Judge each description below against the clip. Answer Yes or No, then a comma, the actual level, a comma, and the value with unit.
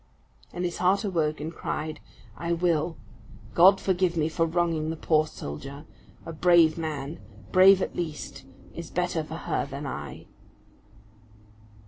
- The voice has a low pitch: No, medium, 165 Hz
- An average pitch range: No, narrow, 2.3 semitones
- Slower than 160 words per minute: Yes, average, 140 wpm